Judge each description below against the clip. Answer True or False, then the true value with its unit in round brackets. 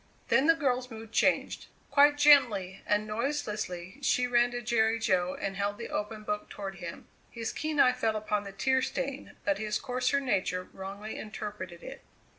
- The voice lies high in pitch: True (220 Hz)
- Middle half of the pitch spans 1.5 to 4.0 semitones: False (4.5 semitones)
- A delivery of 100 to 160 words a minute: False (175 wpm)